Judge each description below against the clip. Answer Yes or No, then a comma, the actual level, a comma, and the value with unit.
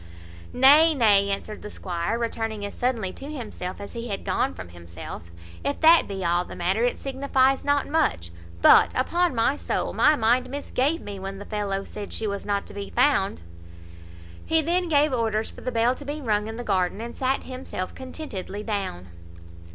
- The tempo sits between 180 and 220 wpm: Yes, average, 190 wpm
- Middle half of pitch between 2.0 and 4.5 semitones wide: No, wide, 5.5 semitones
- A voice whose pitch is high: Yes, high, 225 Hz